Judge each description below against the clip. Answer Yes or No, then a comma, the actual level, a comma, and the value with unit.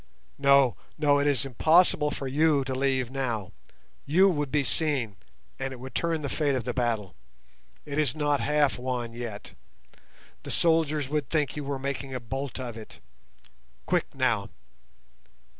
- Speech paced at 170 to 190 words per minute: No, average, 160 wpm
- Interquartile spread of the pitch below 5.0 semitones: Yes, average, 2.7 semitones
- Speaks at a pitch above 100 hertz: Yes, medium, 140 Hz